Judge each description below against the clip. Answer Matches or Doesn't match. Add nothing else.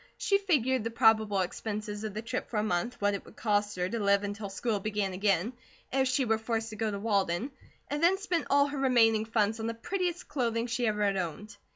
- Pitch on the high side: Matches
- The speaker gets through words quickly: Matches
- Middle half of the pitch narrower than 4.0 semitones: Matches